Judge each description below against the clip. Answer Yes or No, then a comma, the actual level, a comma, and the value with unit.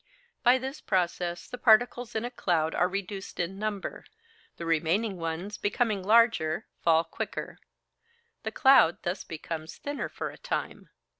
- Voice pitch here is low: No, high, 195 Hz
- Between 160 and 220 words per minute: No, average, 145 wpm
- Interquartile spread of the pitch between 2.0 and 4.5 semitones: No, wide, 5.4 semitones